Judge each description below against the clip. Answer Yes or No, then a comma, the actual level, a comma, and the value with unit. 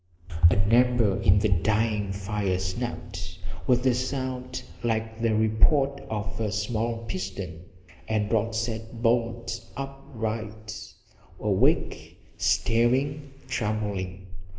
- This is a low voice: Yes, low, 110 Hz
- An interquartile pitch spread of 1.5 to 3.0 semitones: Yes, narrow, 2.6 semitones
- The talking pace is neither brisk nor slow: No, slow, 105 wpm